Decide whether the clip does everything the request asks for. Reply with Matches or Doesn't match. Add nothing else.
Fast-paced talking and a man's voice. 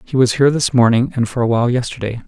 Matches